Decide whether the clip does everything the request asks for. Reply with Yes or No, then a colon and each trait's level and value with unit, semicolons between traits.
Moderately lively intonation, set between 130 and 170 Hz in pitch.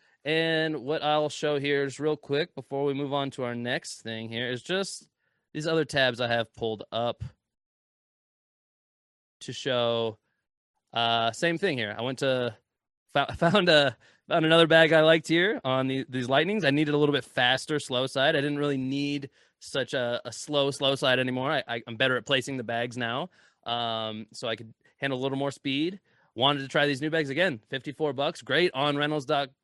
Yes: average, 3.8 semitones; low, 135 Hz